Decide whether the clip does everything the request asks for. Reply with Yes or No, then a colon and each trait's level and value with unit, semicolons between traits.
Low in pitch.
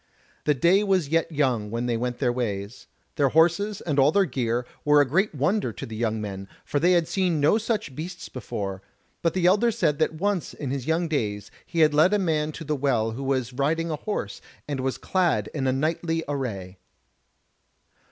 No: medium, 150 Hz